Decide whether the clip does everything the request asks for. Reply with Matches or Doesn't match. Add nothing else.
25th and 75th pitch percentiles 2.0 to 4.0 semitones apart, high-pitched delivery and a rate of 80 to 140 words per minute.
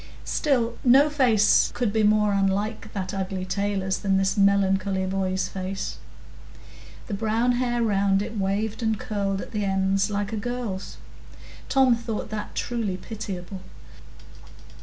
Matches